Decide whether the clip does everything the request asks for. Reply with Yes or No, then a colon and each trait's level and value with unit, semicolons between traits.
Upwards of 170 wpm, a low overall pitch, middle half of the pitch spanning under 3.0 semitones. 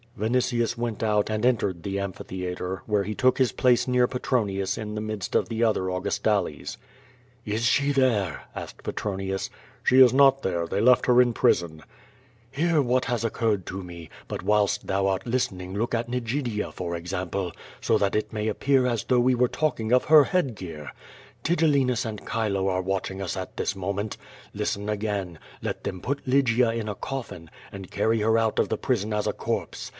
No: average, 190 wpm; low, 110 Hz; average, 4.3 semitones